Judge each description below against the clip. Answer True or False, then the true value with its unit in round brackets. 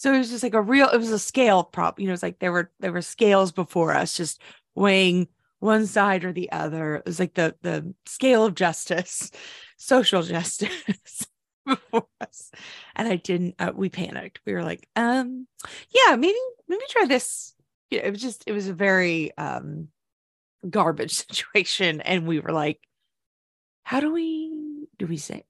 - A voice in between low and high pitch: False (195 Hz)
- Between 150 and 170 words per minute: False (185 wpm)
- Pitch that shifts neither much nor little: False (6.2 semitones)